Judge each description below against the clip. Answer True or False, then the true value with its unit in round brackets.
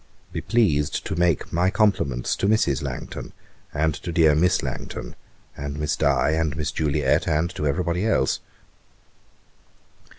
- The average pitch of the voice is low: True (80 Hz)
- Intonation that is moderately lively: True (3.4 semitones)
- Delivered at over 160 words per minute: False (145 wpm)